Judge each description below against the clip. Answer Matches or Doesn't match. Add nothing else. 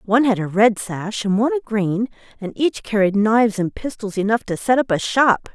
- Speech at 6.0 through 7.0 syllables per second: Doesn't match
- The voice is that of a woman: Matches